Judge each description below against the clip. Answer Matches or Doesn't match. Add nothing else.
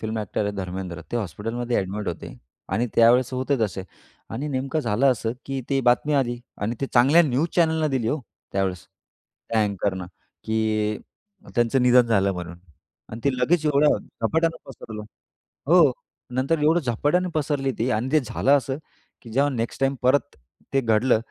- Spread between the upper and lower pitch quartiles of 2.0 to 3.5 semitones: Doesn't match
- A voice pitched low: Matches